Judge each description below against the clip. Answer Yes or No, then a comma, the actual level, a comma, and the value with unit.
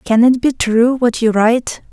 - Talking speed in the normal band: No, fast, 220 wpm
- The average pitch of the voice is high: Yes, high, 235 Hz